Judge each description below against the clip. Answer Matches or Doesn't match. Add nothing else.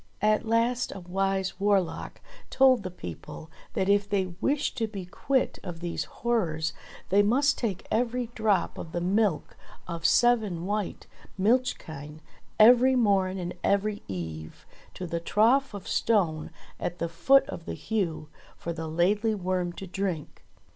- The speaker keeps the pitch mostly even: Doesn't match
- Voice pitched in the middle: Doesn't match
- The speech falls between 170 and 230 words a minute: Doesn't match